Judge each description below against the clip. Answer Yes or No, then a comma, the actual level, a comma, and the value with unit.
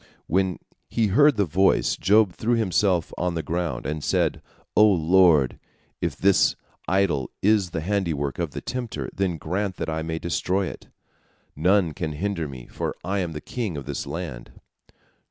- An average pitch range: Yes, average, 4.0 semitones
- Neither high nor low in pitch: No, very low, 90 Hz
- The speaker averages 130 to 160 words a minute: No, average, 170 wpm